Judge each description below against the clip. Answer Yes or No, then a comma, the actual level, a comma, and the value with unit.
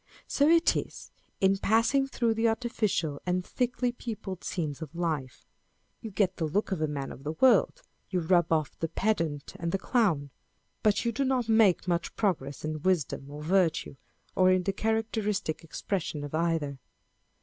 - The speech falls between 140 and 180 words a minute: Yes, average, 170 wpm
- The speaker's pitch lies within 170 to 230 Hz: Yes, medium, 185 Hz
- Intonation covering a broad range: Yes, wide, 6.0 semitones